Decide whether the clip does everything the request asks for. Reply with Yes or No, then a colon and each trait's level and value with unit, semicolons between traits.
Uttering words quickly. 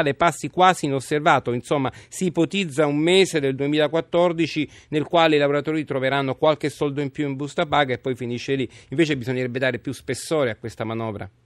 Yes: fast, 180 wpm